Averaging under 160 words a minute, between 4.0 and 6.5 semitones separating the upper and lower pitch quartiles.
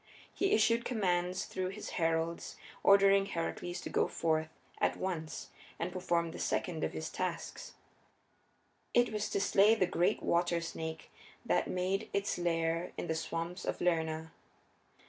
No: average, 145 wpm; average, 3.0 semitones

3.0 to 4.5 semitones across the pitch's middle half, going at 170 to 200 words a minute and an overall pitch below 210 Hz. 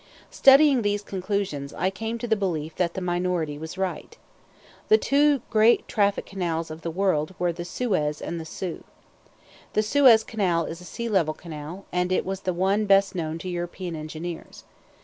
Yes: average, 3.7 semitones; average, 180 wpm; medium, 185 Hz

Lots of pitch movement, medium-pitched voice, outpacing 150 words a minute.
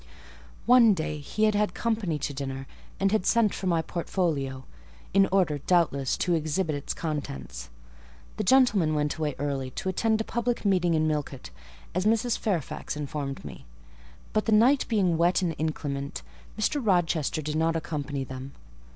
Yes: wide, 6.0 semitones; medium, 165 Hz; average, 160 wpm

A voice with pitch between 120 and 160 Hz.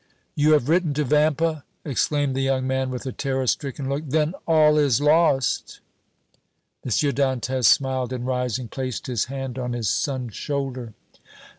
Yes: low, 135 Hz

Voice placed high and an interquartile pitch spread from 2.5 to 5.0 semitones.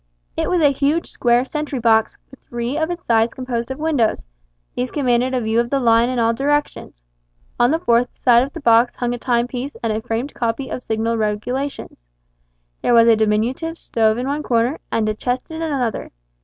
Yes: high, 245 Hz; average, 3.2 semitones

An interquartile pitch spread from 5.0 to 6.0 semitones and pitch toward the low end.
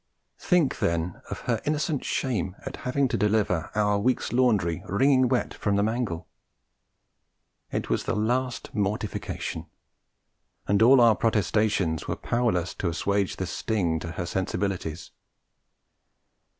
Yes: average, 5.3 semitones; low, 105 Hz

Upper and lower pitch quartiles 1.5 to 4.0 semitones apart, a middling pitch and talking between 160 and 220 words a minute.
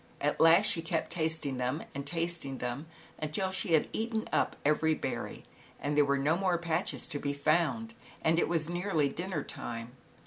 Yes: average, 3.3 semitones; medium, 160 Hz; average, 180 wpm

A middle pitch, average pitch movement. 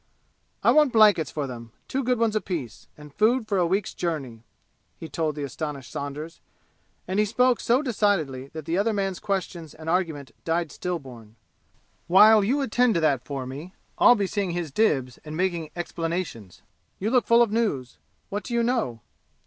No: medium, 175 Hz; wide, 6.8 semitones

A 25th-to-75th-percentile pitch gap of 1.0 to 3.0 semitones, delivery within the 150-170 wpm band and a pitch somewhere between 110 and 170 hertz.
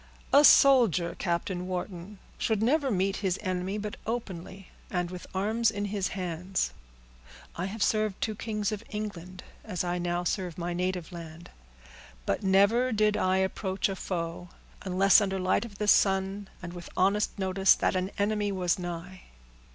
No: average, 2.7 semitones; average, 165 wpm; high, 190 Hz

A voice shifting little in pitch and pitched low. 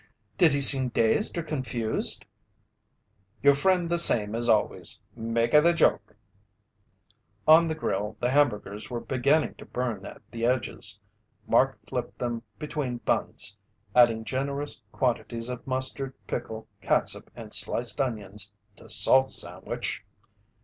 No: average, 3.9 semitones; low, 125 Hz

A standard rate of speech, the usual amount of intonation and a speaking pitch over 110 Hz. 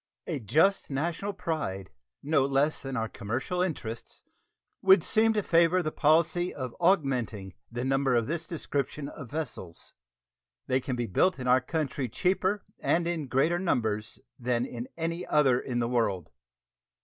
No: average, 155 wpm; wide, 5.7 semitones; medium, 140 Hz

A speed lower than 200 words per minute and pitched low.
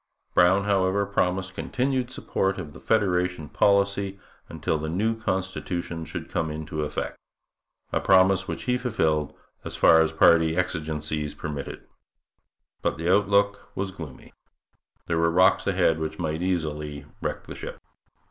Yes: average, 140 wpm; very low, 90 Hz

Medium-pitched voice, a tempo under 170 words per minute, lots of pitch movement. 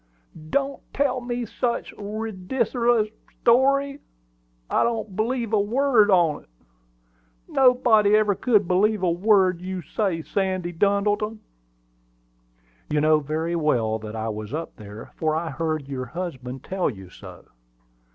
No: high, 195 Hz; slow, 135 wpm; wide, 6.3 semitones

